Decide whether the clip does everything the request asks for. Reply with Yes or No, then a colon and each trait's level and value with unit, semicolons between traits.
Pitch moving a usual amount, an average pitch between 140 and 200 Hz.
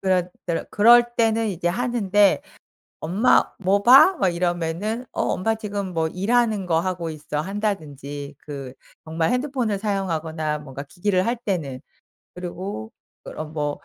Yes: average, 4.9 semitones; medium, 185 Hz